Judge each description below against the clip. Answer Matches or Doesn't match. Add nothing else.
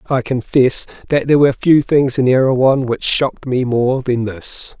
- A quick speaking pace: Doesn't match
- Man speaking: Matches